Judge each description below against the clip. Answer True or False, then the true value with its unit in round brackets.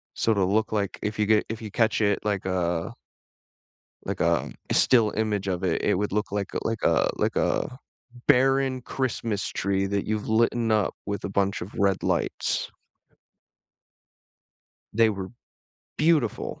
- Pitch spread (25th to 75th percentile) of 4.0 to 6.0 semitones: False (2.4 semitones)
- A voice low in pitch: True (105 Hz)